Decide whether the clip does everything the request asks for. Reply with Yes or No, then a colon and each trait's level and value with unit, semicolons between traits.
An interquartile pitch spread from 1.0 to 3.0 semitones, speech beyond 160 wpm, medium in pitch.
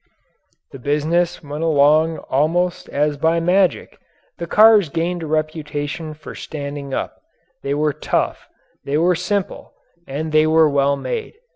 No: average, 2.7 semitones; average, 140 wpm; medium, 155 Hz